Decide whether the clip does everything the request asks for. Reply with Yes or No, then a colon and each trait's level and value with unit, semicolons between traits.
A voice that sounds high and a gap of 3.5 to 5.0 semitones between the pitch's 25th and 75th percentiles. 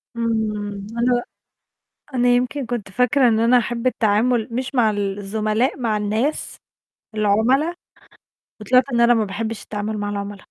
No: high, 225 Hz; average, 2.9 semitones